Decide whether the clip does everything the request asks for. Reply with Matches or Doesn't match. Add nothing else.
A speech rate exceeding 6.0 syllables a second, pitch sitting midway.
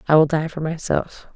Doesn't match